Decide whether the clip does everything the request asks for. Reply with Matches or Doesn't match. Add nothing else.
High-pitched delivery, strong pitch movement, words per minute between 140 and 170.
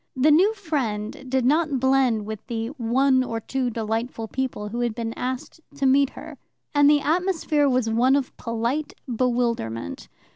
Doesn't match